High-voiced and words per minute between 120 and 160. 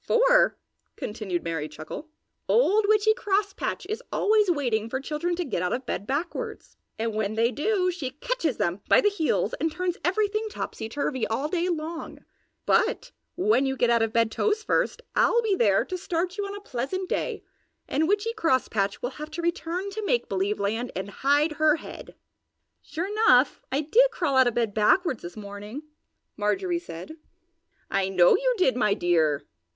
No: very high, 305 Hz; average, 180 wpm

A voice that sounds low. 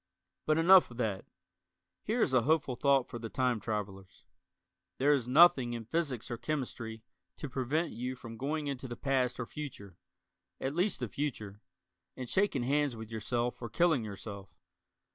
Yes: low, 125 Hz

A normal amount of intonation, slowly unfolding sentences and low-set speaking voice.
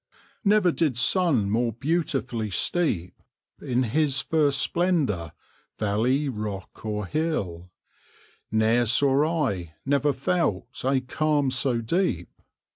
No: wide, 6.2 semitones; slow, 110 wpm; low, 130 Hz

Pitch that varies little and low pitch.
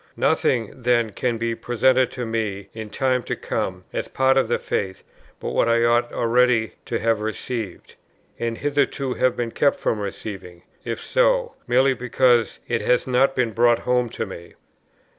Yes: narrow, 2.3 semitones; low, 120 Hz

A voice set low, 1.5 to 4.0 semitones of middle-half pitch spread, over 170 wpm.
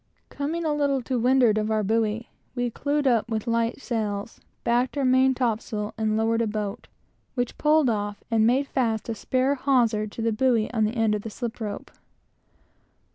No: high, 230 Hz; average, 3.2 semitones; average, 185 wpm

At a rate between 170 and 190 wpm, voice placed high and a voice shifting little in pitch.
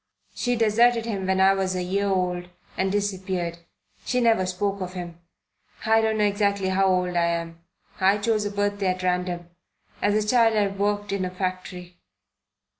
Yes: average, 180 wpm; high, 195 Hz; narrow, 2.2 semitones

